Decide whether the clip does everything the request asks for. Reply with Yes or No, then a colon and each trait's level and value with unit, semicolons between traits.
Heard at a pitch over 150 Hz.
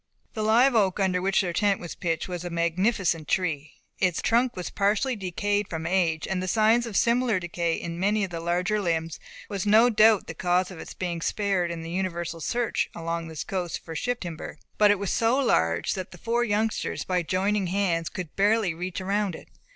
Yes: medium, 185 Hz